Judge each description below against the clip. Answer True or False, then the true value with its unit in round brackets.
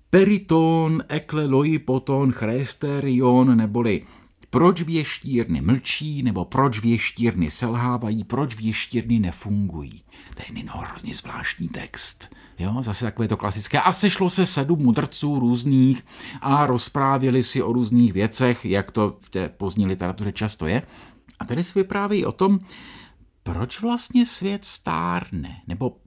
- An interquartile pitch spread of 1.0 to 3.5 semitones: False (5.8 semitones)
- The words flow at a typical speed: True (130 wpm)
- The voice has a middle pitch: False (130 Hz)